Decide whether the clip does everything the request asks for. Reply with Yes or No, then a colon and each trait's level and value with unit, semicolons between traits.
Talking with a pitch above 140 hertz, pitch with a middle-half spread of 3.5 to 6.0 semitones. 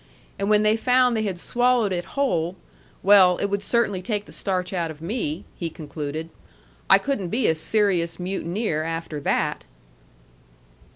Yes: high, 190 Hz; average, 4.6 semitones